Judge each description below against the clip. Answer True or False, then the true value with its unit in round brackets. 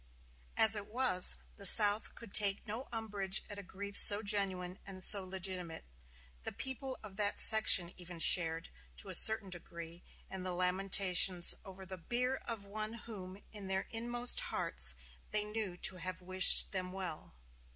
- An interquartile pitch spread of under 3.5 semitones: True (2.8 semitones)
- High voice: True (195 Hz)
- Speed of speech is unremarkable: True (160 wpm)